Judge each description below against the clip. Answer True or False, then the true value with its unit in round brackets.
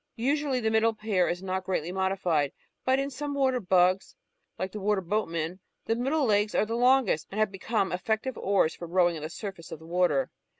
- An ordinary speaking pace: False (210 wpm)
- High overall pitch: True (195 Hz)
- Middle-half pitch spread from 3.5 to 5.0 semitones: True (4.4 semitones)